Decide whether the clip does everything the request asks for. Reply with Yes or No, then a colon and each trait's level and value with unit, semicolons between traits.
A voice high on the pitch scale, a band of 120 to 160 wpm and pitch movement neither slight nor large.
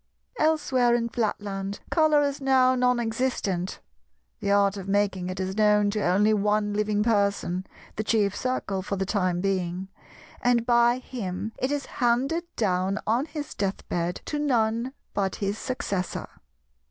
Yes: high, 210 Hz; average, 155 wpm; average, 4.2 semitones